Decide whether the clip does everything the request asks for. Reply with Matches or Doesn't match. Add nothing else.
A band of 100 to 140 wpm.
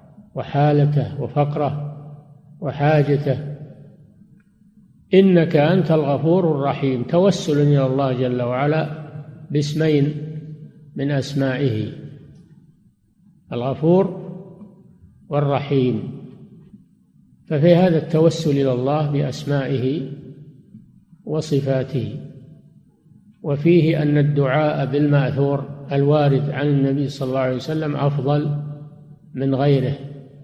Doesn't match